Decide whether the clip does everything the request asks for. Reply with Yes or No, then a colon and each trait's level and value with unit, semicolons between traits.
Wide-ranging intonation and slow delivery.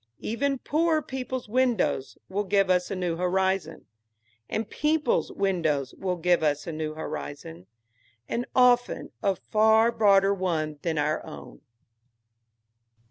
Yes: wide, 6.5 semitones; slow, 130 wpm